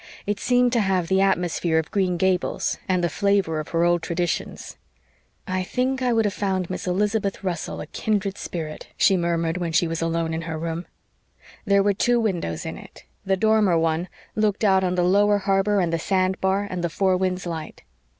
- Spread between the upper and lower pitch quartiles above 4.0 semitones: No, average, 3.0 semitones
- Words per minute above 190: Yes, average, 200 wpm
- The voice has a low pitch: No, medium, 185 Hz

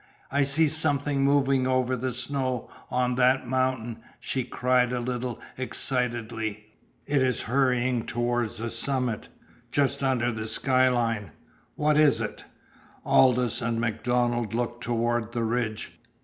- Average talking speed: No, slow, 130 wpm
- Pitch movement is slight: Yes, narrow, 1.8 semitones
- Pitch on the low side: Yes, low, 125 Hz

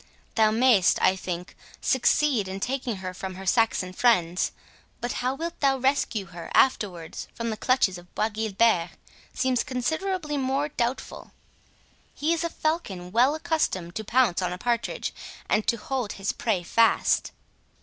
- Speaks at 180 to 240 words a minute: No, average, 150 wpm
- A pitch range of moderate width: No, wide, 5.8 semitones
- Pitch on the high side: Yes, high, 230 Hz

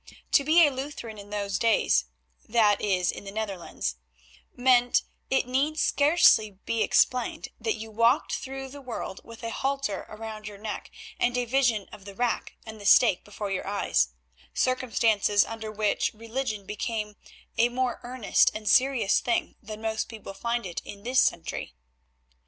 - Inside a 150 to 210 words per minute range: Yes, average, 160 wpm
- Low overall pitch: No, high, 225 Hz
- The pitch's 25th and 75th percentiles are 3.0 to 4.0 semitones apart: Yes, average, 3.6 semitones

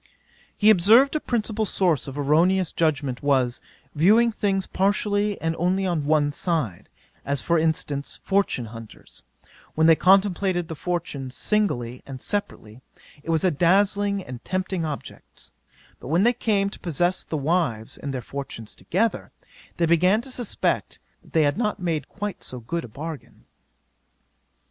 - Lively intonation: Yes, wide, 5.7 semitones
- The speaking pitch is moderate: Yes, medium, 170 Hz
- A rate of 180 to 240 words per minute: No, average, 155 wpm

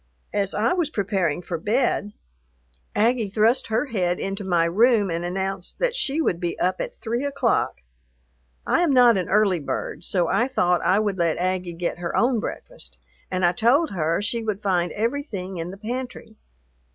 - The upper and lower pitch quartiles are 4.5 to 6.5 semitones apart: Yes, average, 4.8 semitones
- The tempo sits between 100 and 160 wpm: No, average, 180 wpm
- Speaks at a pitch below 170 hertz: No, high, 200 Hz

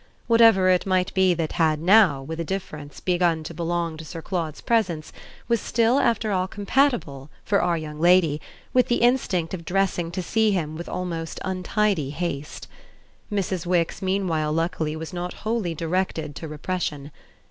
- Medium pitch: Yes, medium, 175 Hz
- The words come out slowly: No, average, 165 wpm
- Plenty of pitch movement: No, average, 3.4 semitones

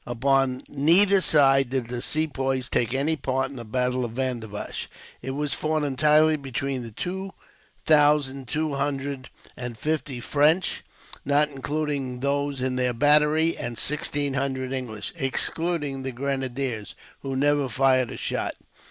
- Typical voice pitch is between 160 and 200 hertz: No, low, 135 Hz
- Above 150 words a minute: No, average, 145 wpm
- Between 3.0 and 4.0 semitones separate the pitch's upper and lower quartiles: No, narrow, 2.6 semitones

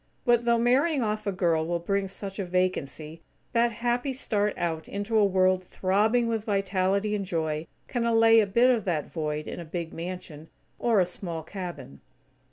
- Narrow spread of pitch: No, average, 4.7 semitones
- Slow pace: No, average, 180 wpm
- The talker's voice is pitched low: No, high, 195 Hz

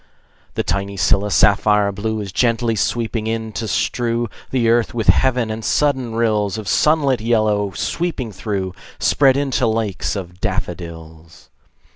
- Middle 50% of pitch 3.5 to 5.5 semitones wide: No, average, 3.1 semitones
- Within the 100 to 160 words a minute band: Yes, average, 140 wpm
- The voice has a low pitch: Yes, low, 110 Hz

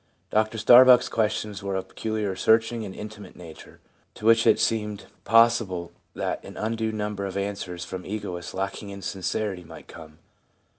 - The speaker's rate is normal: Yes, average, 160 wpm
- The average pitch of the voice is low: Yes, low, 105 Hz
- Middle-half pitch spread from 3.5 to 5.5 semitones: No, average, 2.8 semitones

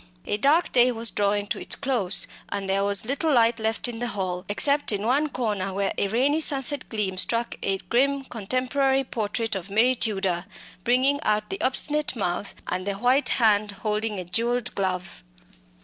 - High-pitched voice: Yes, high, 225 Hz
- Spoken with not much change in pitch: No, average, 4.3 semitones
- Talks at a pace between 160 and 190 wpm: Yes, average, 180 wpm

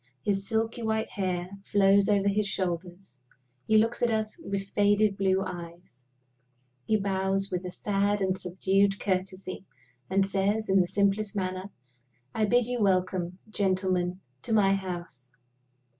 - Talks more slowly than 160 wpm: Yes, average, 145 wpm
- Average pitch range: No, narrow, 1.8 semitones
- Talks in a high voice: Yes, high, 195 Hz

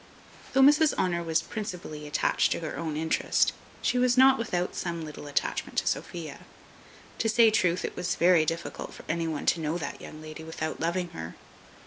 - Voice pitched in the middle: Yes, medium, 170 Hz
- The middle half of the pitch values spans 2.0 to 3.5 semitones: No, average, 4.8 semitones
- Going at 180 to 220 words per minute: Yes, average, 185 wpm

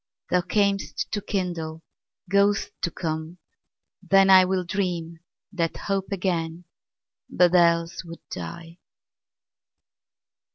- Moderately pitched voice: Yes, medium, 175 Hz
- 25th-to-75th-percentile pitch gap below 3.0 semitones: Yes, narrow, 2.5 semitones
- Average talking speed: No, slow, 95 wpm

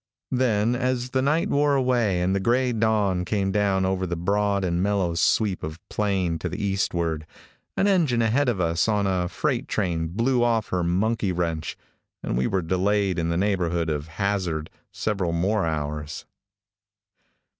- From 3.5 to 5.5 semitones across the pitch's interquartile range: Yes, average, 4.4 semitones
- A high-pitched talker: No, very low, 95 Hz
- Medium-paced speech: Yes, average, 165 wpm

